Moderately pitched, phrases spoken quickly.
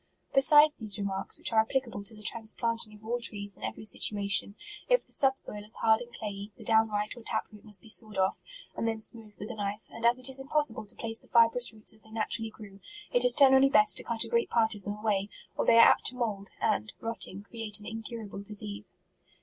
No: high, 220 Hz; fast, 240 wpm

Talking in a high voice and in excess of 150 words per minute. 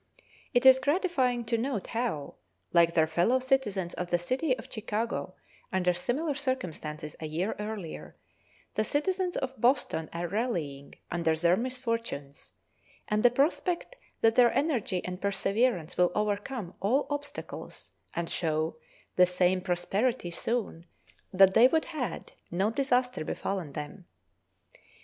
No: high, 210 Hz; slow, 135 wpm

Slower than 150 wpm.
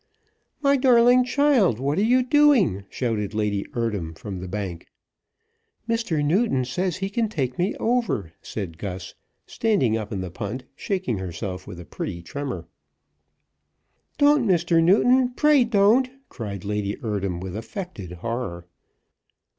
Yes: average, 140 wpm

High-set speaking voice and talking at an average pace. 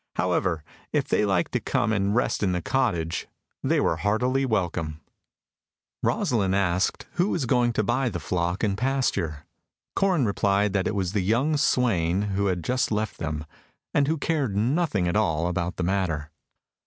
No: low, 100 Hz; average, 170 wpm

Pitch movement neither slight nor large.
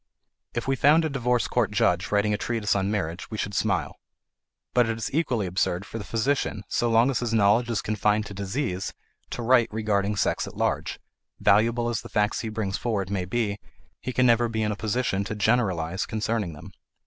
Yes: average, 3.0 semitones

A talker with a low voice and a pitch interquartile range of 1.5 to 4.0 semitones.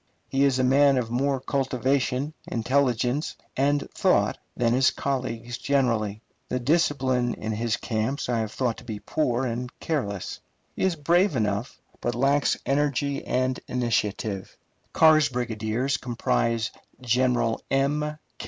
Yes: low, 125 Hz; average, 3.1 semitones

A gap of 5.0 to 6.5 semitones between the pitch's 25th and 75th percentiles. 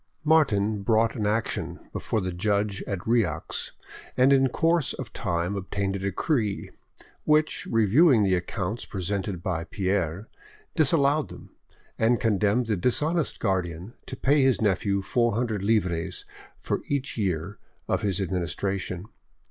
No: average, 4.4 semitones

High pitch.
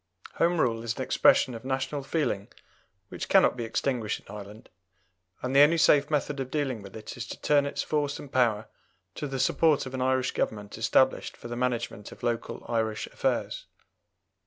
No: low, 130 Hz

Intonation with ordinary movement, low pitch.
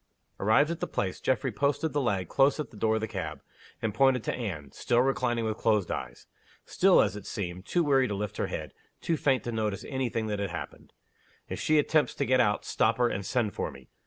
Yes: average, 4.8 semitones; low, 115 Hz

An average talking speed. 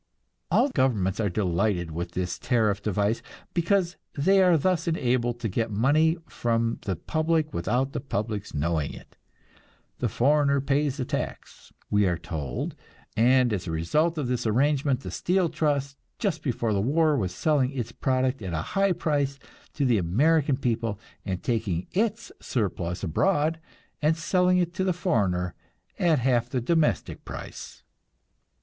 Yes: average, 155 wpm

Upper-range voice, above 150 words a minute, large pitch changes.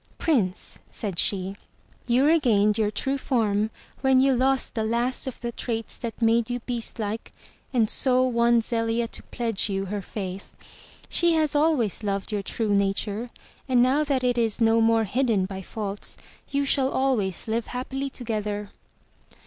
No: high, 230 Hz; average, 160 wpm; average, 3.7 semitones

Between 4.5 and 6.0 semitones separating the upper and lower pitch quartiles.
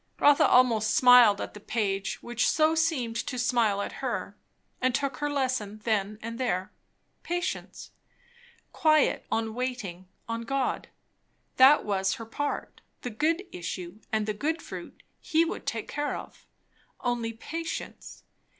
Yes: average, 5.0 semitones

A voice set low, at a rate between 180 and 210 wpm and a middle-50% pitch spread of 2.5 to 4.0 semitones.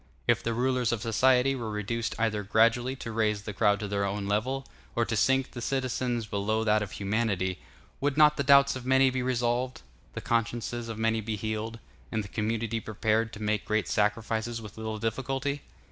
Yes: low, 115 Hz; average, 190 wpm; average, 2.8 semitones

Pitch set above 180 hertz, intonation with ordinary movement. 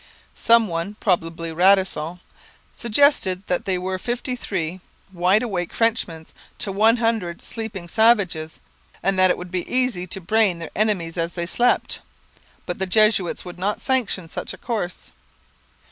Yes: high, 190 Hz; average, 4.1 semitones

